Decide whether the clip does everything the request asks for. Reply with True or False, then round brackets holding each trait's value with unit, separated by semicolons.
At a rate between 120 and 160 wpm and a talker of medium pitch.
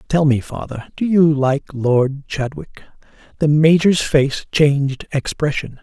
True (135 wpm; 145 Hz)